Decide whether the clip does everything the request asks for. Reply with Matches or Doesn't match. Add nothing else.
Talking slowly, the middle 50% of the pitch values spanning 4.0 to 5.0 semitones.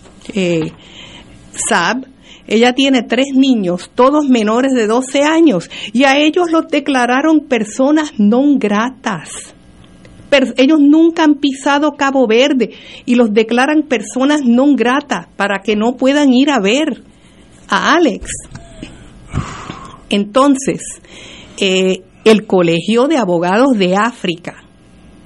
Matches